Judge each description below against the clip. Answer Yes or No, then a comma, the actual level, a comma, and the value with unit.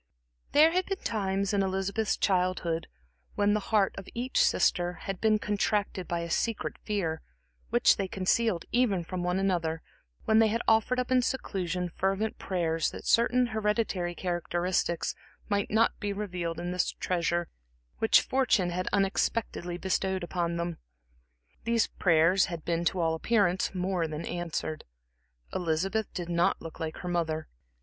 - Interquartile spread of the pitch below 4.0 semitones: Yes, average, 3.4 semitones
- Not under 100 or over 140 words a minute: No, average, 155 wpm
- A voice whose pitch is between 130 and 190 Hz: Yes, medium, 185 Hz